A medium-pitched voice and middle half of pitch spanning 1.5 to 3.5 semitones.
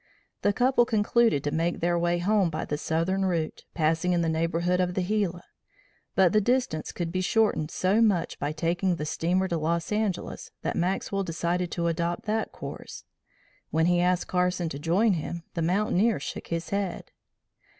Yes: medium, 175 Hz; average, 2.8 semitones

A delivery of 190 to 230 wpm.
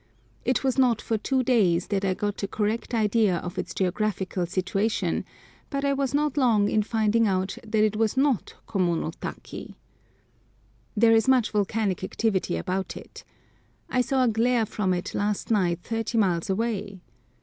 No: average, 165 wpm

